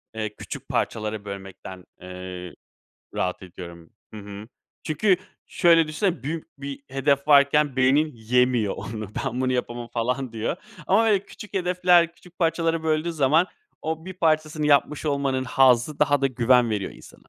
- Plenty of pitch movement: Yes, wide, 6.1 semitones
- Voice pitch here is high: No, low, 135 Hz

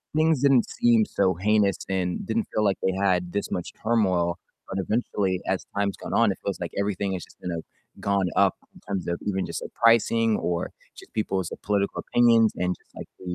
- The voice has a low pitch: Yes, low, 100 Hz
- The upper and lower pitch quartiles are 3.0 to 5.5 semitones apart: Yes, average, 3.3 semitones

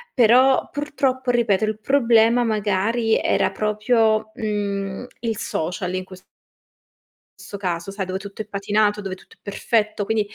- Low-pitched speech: No, high, 215 Hz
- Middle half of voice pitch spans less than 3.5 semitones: Yes, average, 2.7 semitones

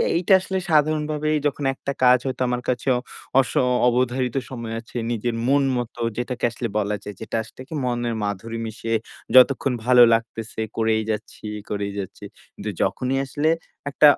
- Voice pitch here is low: Yes, low, 125 Hz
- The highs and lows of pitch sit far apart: No, average, 3.3 semitones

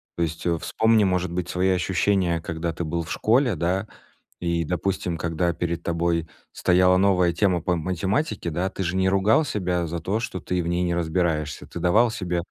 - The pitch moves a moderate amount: No, narrow, 1.9 semitones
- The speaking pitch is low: Yes, very low, 90 Hz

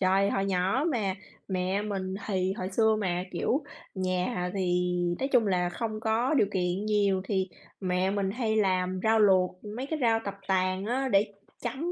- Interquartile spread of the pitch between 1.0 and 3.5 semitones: Yes, average, 3.0 semitones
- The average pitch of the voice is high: Yes, high, 195 Hz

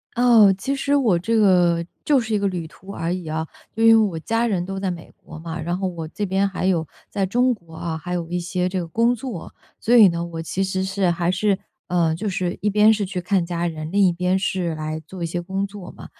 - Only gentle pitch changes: No, average, 3.1 semitones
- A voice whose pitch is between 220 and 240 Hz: No, medium, 185 Hz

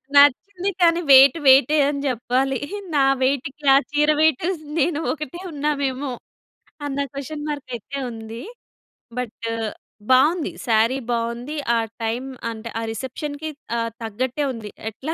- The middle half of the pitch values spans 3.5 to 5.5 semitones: Yes, average, 3.9 semitones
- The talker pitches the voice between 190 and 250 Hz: No, very high, 270 Hz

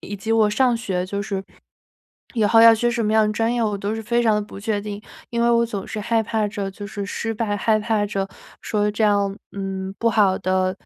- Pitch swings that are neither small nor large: No, narrow, 2.0 semitones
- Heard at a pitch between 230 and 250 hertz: No, high, 210 Hz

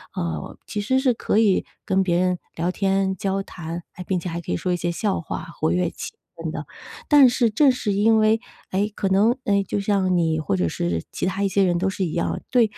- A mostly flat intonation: No, average, 3.2 semitones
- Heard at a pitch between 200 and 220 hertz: No, high, 190 Hz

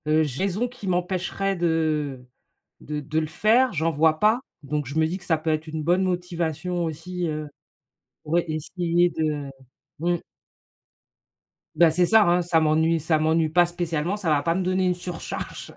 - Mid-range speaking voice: Yes, medium, 165 Hz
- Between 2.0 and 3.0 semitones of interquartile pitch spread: Yes, narrow, 2.4 semitones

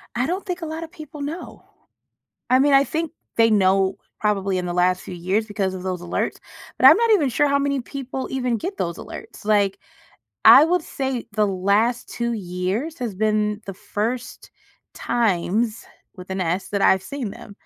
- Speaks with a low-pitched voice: No, high, 220 Hz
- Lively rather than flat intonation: Yes, wide, 6.4 semitones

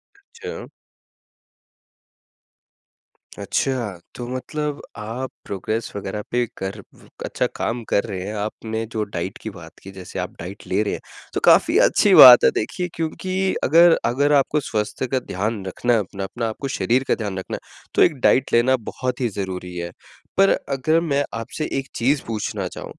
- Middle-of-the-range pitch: No, low, 115 Hz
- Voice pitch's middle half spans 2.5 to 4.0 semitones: No, wide, 5.4 semitones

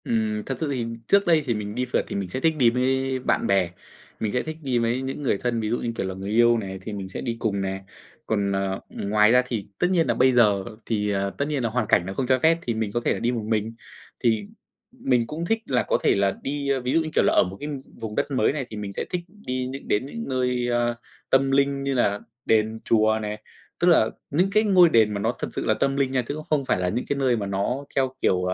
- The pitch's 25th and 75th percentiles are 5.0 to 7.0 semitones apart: No, average, 4.4 semitones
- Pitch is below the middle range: Yes, low, 120 Hz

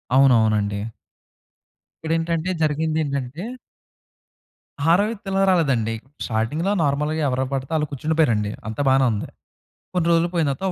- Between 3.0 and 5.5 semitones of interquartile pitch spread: Yes, average, 4.5 semitones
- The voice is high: No, medium, 150 Hz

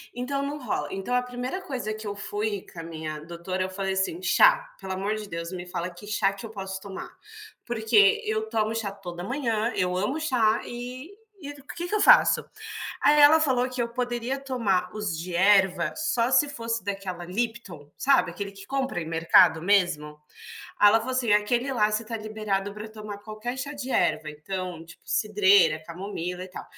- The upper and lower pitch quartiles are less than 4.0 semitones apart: No, average, 4.8 semitones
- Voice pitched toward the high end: Yes, high, 210 Hz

